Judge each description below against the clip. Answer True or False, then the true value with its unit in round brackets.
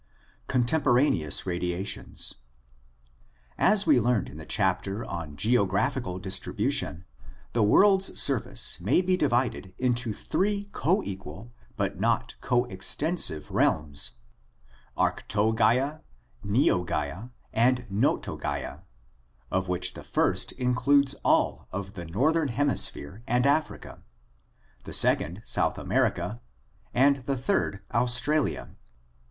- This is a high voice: False (115 Hz)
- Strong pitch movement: True (6.6 semitones)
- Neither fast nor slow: False (100 wpm)